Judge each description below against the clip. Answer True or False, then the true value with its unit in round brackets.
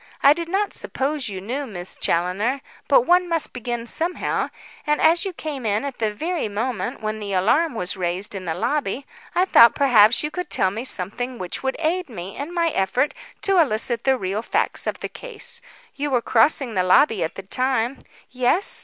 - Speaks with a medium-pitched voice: False (250 Hz)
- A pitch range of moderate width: False (6.9 semitones)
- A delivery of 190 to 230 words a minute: True (200 wpm)